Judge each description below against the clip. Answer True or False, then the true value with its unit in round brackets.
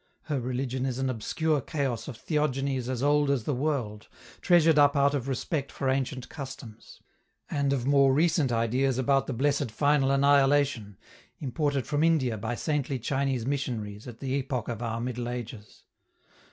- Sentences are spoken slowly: False (165 wpm)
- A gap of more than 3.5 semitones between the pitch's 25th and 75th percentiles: False (2.8 semitones)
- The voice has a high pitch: False (135 Hz)